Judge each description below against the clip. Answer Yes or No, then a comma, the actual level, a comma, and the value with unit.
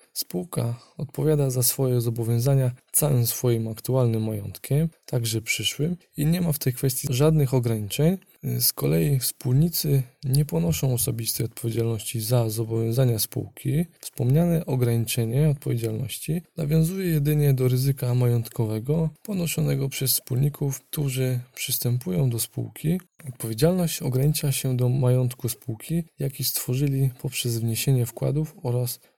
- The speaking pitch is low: Yes, low, 130 Hz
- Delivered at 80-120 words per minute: Yes, average, 115 wpm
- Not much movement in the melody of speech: No, average, 3.9 semitones